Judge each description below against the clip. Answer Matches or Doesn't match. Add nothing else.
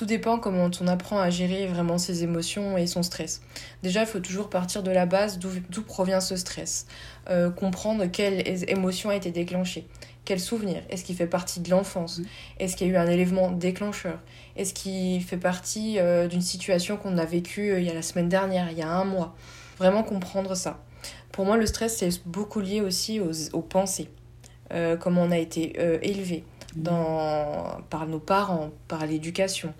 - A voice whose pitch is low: Doesn't match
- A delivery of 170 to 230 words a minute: Matches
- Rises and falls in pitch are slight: Matches